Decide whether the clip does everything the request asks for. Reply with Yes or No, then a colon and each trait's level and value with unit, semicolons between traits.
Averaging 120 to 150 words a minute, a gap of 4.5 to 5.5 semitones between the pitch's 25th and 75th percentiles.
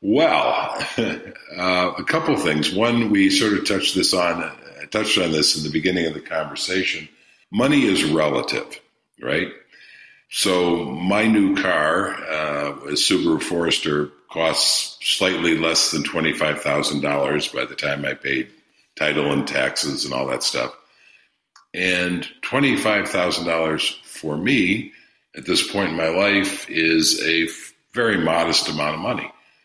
No: average, 140 wpm; average, 3.6 semitones